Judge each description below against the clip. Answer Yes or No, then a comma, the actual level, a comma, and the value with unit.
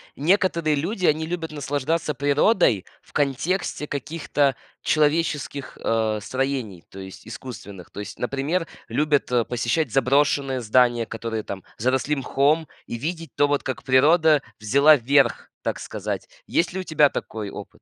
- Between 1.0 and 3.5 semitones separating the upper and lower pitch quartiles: No, average, 4.2 semitones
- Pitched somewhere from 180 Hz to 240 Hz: No, medium, 140 Hz